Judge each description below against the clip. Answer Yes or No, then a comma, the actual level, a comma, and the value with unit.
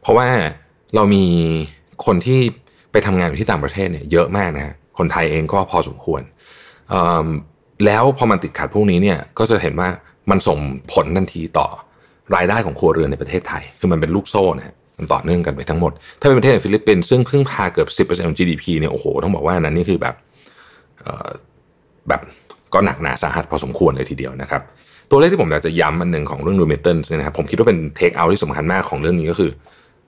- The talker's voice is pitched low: Yes, very low, 85 Hz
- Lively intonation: No, average, 4.3 semitones